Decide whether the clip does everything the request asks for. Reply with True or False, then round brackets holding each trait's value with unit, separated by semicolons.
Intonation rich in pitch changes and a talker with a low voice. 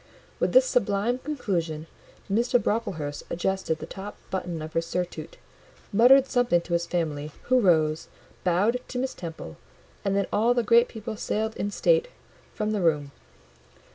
False (6.0 semitones; 195 Hz)